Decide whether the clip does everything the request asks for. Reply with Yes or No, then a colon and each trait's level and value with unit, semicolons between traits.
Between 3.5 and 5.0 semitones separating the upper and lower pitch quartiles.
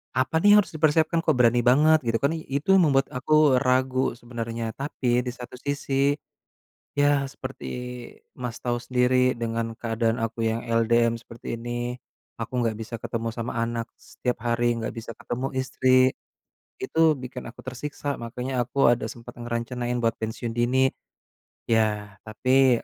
No: narrow, 2.4 semitones